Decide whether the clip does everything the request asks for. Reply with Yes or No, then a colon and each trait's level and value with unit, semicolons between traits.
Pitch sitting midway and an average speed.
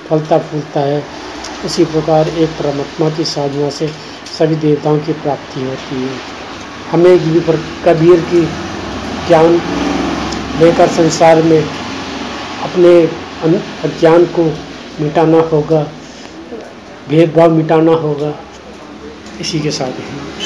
No: medium, 160 Hz; slow, 105 wpm